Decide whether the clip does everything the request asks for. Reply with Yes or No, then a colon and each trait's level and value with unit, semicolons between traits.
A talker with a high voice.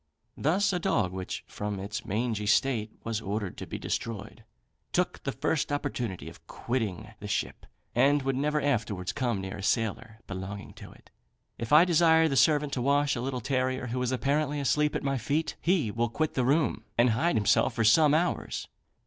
No: low, 125 Hz